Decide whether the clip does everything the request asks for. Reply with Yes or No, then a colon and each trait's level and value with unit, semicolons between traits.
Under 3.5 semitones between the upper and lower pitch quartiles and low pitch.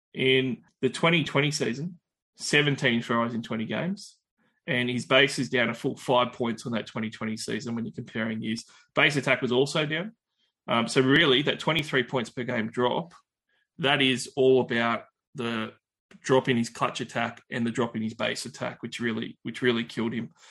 Yes: average, 2.9 semitones; low, 125 Hz